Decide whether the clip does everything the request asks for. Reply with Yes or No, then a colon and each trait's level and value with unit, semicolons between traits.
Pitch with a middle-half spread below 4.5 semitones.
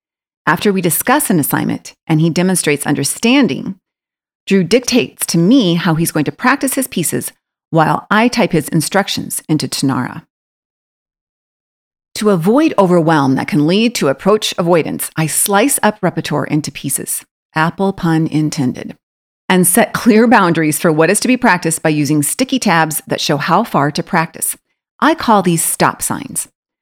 No: wide, 5.4 semitones